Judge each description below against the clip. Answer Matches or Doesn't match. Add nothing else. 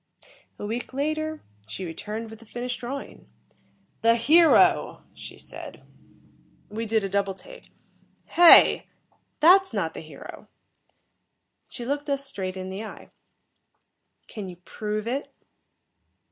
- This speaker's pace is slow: Matches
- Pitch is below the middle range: Doesn't match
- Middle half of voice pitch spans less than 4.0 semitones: Doesn't match